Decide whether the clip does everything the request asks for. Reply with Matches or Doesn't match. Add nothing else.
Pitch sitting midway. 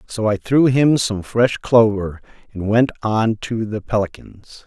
Doesn't match